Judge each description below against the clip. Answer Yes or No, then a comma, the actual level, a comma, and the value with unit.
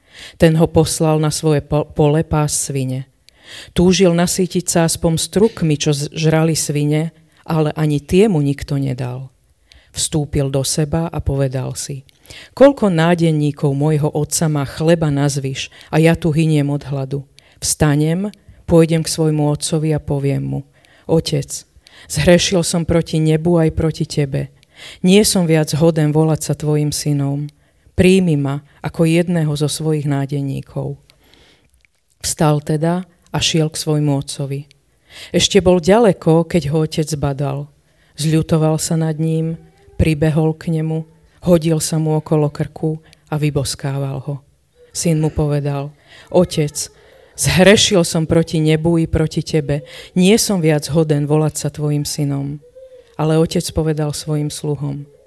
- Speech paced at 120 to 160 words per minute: Yes, average, 135 wpm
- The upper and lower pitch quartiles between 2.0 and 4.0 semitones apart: Yes, narrow, 2.4 semitones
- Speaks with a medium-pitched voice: Yes, medium, 155 Hz